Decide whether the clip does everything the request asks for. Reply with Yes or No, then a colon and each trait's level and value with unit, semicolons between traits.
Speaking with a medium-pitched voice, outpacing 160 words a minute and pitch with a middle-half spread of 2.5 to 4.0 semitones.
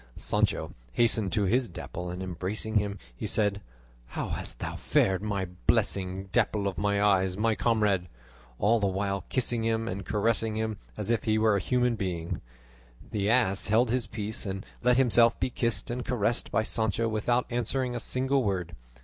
No: low, 110 Hz; average, 175 wpm; average, 3.1 semitones